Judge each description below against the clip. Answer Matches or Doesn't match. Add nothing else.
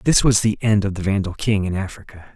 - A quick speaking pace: Matches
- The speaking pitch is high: Doesn't match